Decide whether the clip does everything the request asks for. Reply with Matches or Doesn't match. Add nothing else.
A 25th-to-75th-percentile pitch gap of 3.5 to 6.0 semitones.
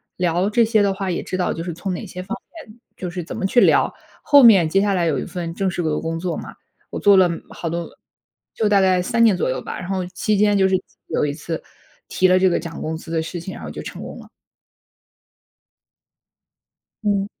Doesn't match